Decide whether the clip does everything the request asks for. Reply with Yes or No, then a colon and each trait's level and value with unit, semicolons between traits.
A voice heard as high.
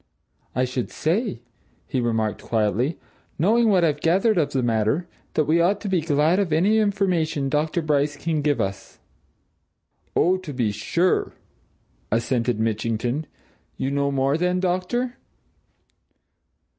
No: medium, 150 Hz